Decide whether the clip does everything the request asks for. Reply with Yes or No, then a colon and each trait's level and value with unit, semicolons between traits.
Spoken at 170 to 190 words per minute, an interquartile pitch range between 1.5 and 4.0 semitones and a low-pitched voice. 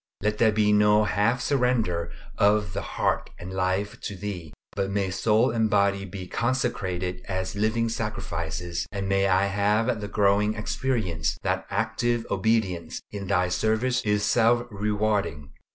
No: average, 150 wpm; average, 2.8 semitones; low, 105 Hz